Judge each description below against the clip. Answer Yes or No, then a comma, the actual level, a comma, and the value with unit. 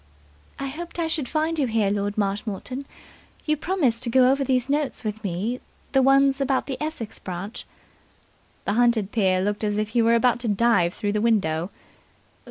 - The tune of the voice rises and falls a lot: No, average, 4.8 semitones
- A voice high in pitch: Yes, high, 235 Hz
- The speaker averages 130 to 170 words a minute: No, average, 185 wpm